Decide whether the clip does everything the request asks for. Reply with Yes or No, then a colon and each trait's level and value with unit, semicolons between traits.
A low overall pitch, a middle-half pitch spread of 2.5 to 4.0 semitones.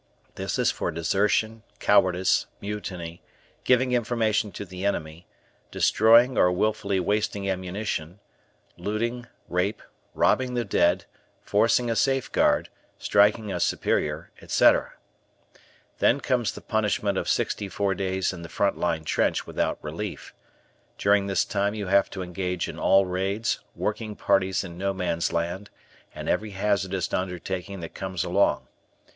Yes: low, 100 Hz; average, 2.9 semitones